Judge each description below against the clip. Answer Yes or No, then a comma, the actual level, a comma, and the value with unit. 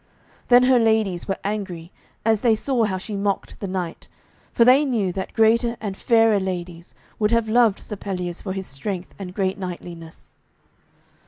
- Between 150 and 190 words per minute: Yes, average, 170 wpm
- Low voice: No, high, 200 Hz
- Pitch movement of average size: Yes, average, 3.6 semitones